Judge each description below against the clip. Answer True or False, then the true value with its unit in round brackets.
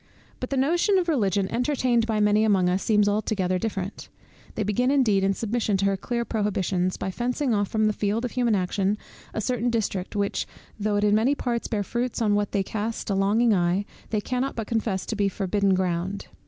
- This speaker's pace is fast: True (210 wpm)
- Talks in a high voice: True (210 Hz)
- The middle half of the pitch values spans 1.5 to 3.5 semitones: True (3.2 semitones)